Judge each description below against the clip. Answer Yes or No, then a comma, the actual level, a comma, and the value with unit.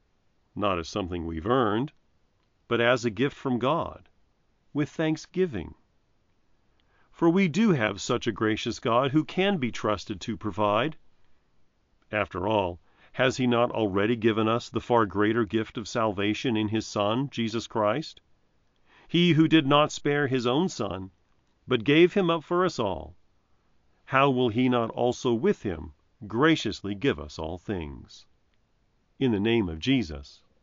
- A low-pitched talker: Yes, low, 115 Hz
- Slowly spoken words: No, average, 155 wpm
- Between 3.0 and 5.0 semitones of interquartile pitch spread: Yes, average, 4.7 semitones